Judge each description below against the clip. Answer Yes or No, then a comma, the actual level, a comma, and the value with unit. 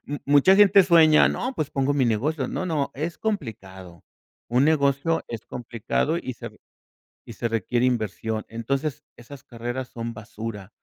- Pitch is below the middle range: Yes, low, 130 Hz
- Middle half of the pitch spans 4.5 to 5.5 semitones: Yes, average, 5.1 semitones